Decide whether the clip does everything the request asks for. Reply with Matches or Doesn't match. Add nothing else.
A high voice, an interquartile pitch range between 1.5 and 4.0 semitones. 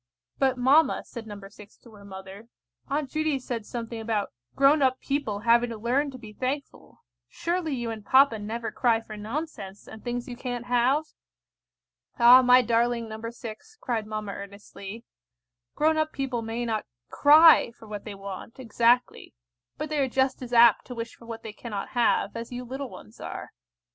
Matches